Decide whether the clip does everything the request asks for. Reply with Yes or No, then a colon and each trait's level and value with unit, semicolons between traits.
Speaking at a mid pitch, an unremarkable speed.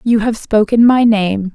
No: high, 220 Hz; average, 195 wpm